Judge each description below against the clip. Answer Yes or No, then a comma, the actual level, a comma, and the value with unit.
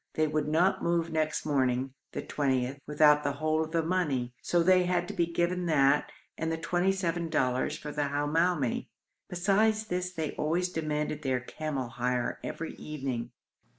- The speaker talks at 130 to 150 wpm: No, average, 170 wpm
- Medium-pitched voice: Yes, medium, 155 Hz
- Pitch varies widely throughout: No, average, 3.5 semitones